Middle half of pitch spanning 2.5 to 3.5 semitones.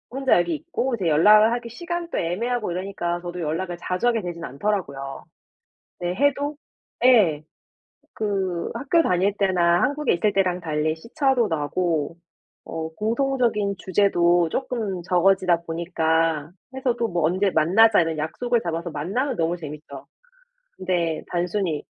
No: wide, 5.6 semitones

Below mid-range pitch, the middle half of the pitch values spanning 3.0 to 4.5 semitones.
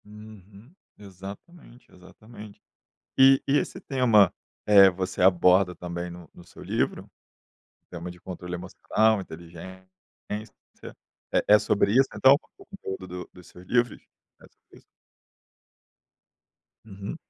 Yes: very low, 95 Hz; average, 3.4 semitones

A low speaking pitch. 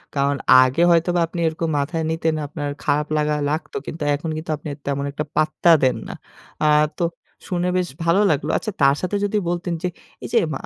No: medium, 160 Hz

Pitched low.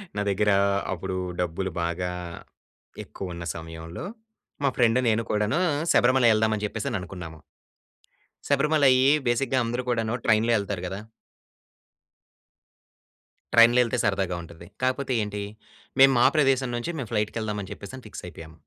Yes: low, 110 Hz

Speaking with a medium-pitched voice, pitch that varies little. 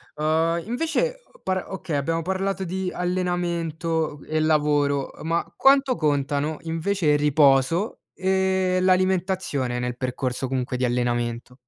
No: medium, 165 Hz; average, 4.8 semitones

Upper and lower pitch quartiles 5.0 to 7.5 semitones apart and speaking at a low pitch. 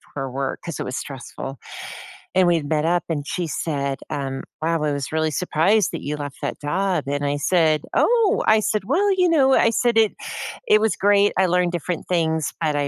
No: wide, 5.6 semitones; medium, 165 Hz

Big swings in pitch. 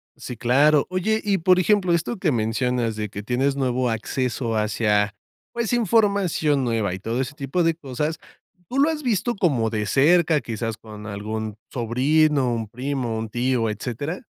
Yes: wide, 6.7 semitones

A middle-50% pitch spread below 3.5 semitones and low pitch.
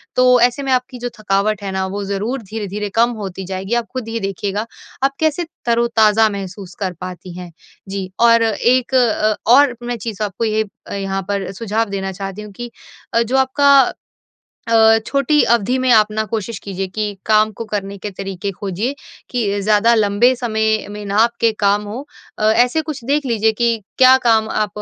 No: average, 3.1 semitones; high, 215 Hz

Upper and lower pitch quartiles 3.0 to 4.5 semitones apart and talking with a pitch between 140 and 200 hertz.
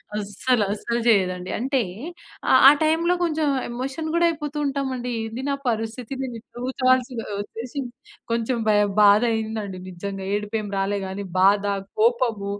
No: average, 4.2 semitones; high, 230 Hz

